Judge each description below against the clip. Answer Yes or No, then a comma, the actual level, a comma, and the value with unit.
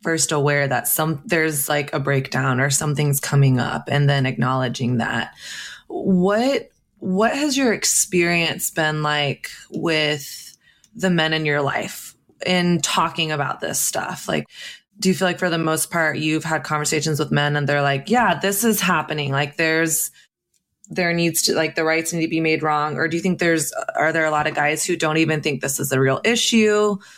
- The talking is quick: No, average, 195 wpm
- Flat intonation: No, average, 3.2 semitones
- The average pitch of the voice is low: No, medium, 155 Hz